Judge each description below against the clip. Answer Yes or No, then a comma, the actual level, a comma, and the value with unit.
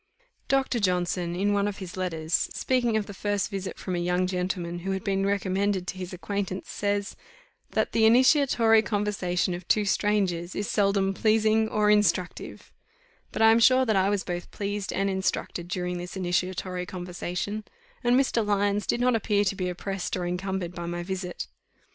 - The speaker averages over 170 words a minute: Yes, average, 180 wpm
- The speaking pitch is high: Yes, high, 195 Hz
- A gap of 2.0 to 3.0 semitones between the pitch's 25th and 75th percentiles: Yes, narrow, 2.5 semitones